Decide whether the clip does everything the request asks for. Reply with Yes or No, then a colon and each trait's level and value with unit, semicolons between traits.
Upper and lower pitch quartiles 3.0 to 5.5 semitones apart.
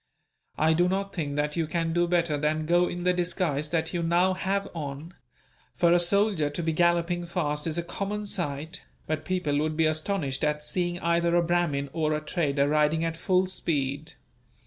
No: narrow, 2.5 semitones